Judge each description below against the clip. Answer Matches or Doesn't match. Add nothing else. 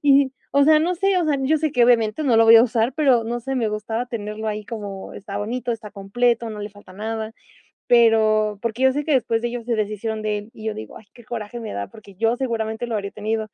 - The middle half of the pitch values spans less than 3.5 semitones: Matches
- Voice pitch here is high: Matches